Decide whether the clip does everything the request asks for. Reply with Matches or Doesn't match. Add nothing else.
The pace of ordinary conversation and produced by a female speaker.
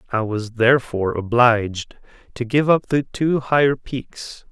Doesn't match